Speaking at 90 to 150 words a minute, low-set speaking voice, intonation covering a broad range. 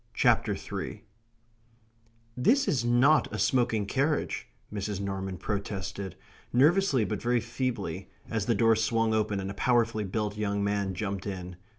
No: average, 145 wpm; low, 110 Hz; average, 3.4 semitones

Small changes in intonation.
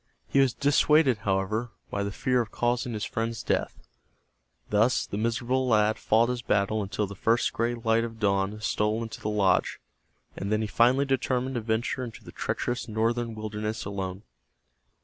Yes: narrow, 2.3 semitones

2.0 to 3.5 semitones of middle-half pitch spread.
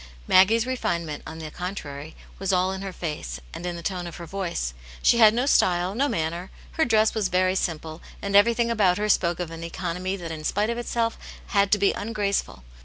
No: average, 3.9 semitones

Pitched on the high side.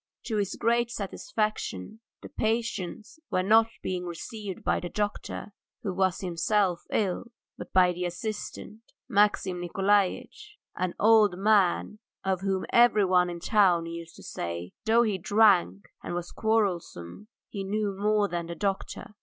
Yes: high, 195 Hz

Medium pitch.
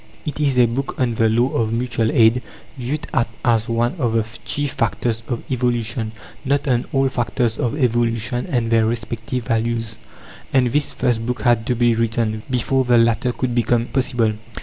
No: low, 120 Hz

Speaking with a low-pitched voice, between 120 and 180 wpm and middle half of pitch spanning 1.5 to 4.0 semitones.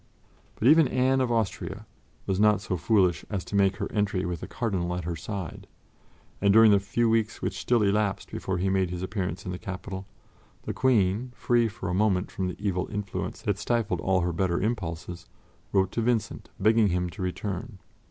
No: low, 100 Hz; average, 195 wpm; average, 3.2 semitones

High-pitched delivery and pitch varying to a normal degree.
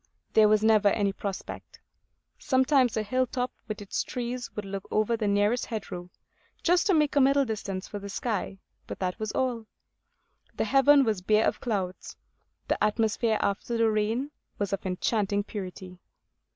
Yes: high, 215 Hz; average, 3.5 semitones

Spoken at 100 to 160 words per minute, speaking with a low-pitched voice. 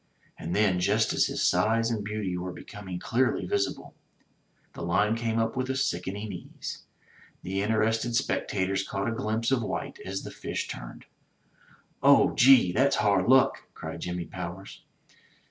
Yes: average, 155 wpm; low, 105 Hz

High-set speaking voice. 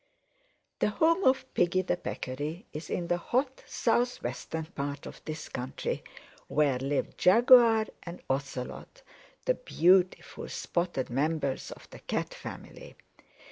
No: medium, 175 Hz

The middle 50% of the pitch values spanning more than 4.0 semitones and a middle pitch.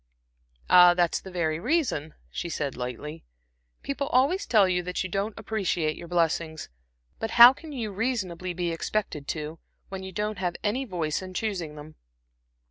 Yes: average, 4.8 semitones; medium, 180 Hz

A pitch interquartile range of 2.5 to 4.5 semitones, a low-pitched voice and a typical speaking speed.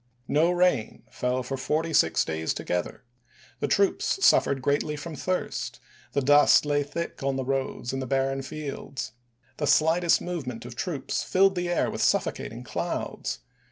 No: average, 4.2 semitones; medium, 145 Hz; average, 155 wpm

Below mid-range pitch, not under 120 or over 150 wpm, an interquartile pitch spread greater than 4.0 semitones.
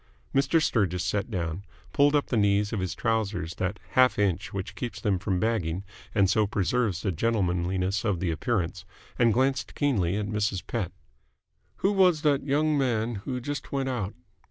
No: low, 105 Hz; average, 175 wpm; average, 5.3 semitones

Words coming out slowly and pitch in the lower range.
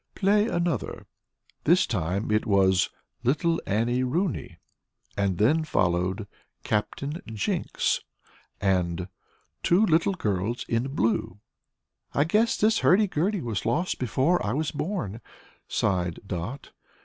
Yes: slow, 120 wpm; low, 120 Hz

